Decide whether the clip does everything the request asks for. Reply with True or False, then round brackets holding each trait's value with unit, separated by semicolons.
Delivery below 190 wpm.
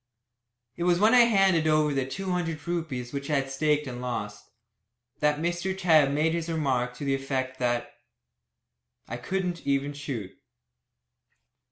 True (155 wpm)